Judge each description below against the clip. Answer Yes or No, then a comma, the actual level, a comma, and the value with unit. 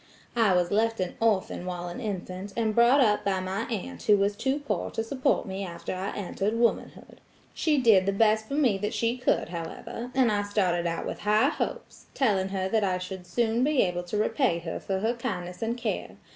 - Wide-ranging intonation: No, average, 3.7 semitones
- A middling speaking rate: No, fast, 215 wpm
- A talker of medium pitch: No, high, 205 Hz